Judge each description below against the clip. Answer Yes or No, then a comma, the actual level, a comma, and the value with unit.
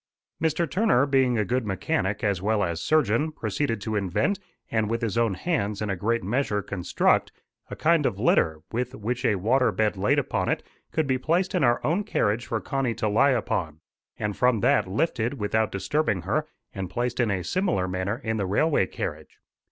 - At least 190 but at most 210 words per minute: Yes, average, 195 wpm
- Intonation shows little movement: No, average, 5.0 semitones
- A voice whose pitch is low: Yes, low, 115 Hz